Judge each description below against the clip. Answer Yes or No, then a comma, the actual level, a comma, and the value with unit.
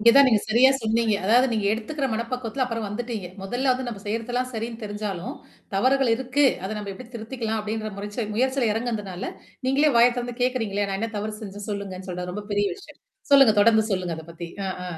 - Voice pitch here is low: No, high, 225 Hz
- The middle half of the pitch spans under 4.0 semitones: Yes, average, 3.3 semitones